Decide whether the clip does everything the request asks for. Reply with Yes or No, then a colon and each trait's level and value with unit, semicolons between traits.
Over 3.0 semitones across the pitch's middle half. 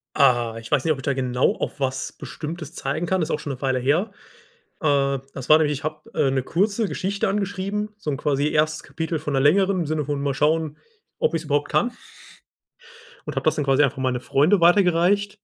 Yes: average, 4.2 semitones